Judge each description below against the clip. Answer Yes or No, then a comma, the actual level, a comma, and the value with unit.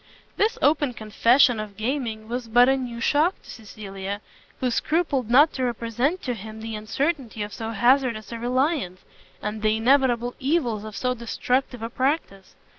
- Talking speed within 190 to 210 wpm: No, average, 165 wpm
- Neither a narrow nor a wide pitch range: Yes, average, 3.5 semitones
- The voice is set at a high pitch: Yes, high, 240 Hz